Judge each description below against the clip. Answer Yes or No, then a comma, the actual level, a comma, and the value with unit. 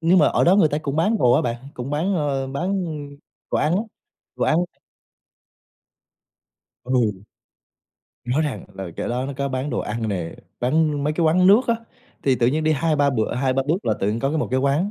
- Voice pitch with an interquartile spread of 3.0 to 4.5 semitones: Yes, average, 4.2 semitones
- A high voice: No, medium, 140 Hz